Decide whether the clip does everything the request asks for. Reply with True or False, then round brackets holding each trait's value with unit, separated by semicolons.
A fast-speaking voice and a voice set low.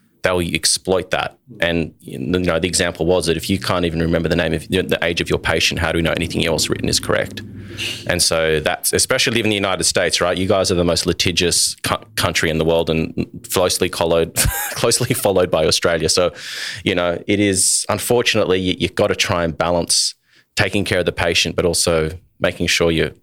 True (215 wpm; 90 Hz)